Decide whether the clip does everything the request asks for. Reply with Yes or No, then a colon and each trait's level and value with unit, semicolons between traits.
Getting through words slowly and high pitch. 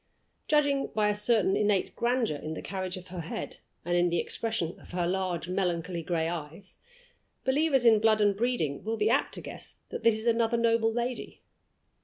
No: average, 190 wpm; high, 210 Hz